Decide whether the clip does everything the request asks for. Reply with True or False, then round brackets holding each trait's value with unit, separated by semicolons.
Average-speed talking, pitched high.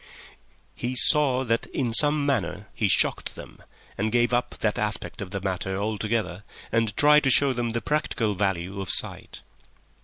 False (165 wpm; 115 Hz)